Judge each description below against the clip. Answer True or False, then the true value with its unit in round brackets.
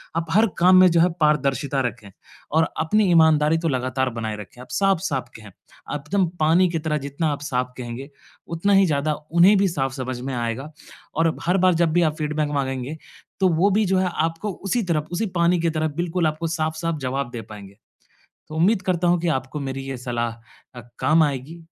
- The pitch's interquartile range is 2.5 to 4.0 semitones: False (4.6 semitones)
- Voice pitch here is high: False (155 Hz)